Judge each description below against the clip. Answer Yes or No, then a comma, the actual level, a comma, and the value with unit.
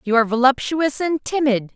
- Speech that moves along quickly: No, average, 170 wpm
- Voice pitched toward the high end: Yes, very high, 265 Hz